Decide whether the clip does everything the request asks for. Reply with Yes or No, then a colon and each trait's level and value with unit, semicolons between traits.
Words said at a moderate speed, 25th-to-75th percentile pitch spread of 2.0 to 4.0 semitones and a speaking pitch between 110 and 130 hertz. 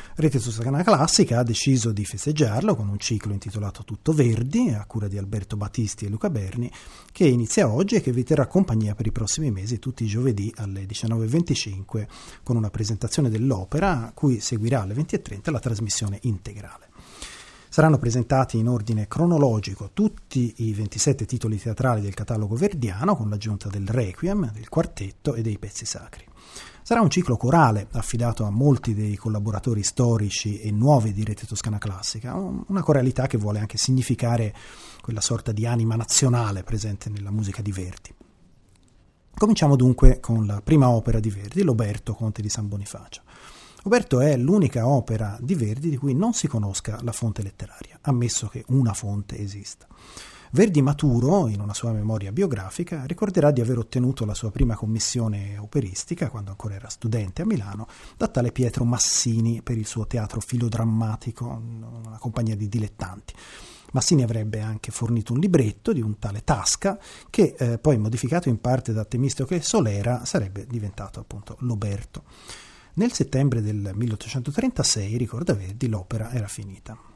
Yes: average, 160 wpm; average, 3.6 semitones; low, 115 Hz